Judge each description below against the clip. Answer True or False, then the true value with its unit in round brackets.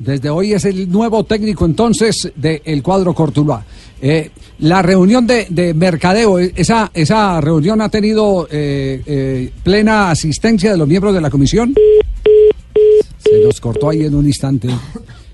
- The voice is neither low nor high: True (180 Hz)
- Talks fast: False (155 wpm)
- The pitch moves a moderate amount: False (6.4 semitones)